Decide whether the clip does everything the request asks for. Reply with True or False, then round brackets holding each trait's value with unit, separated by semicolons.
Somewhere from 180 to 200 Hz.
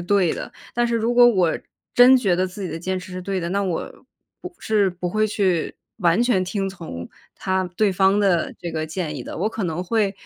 True (190 Hz)